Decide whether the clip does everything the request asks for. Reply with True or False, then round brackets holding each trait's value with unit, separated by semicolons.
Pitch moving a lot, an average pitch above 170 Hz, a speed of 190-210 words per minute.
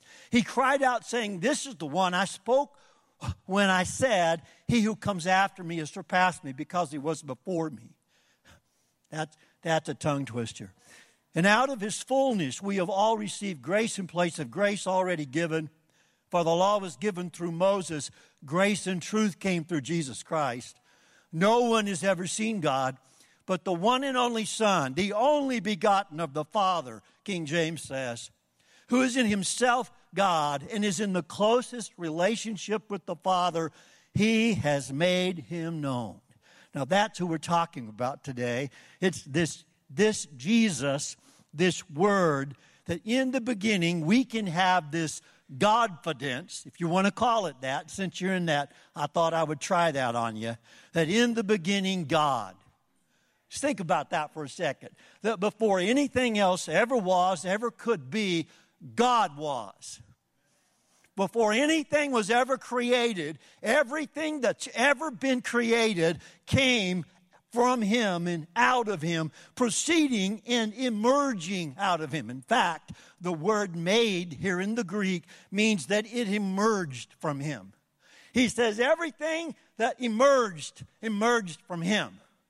False (5.7 semitones; 190 Hz; 155 wpm)